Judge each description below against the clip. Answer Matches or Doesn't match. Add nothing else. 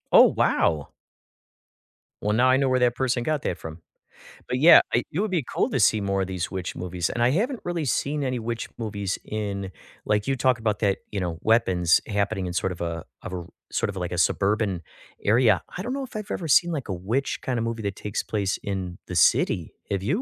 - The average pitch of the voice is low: Matches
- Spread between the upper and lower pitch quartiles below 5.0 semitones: Doesn't match